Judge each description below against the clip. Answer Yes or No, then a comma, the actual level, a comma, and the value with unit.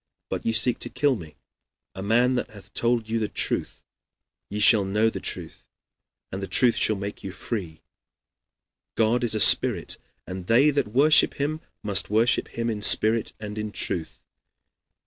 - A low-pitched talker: Yes, low, 110 Hz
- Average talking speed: Yes, average, 170 wpm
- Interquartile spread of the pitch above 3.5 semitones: No, average, 2.9 semitones